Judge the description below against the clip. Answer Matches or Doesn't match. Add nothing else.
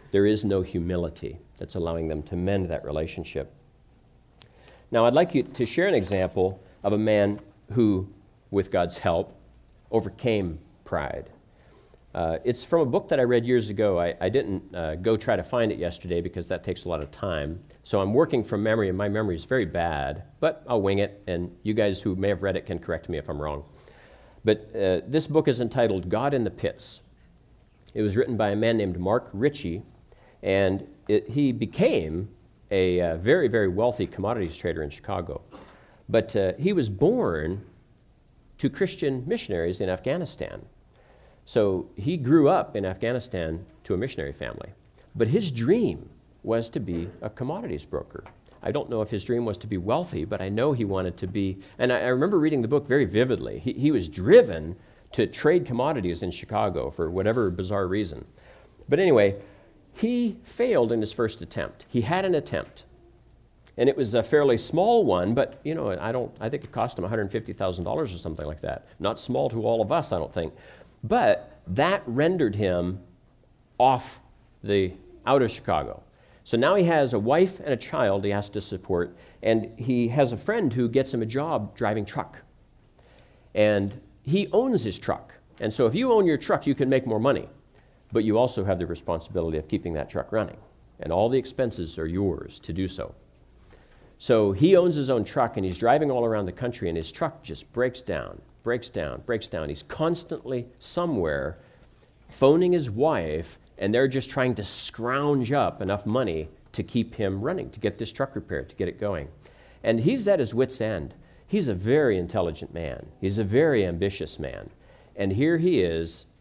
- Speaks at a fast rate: Doesn't match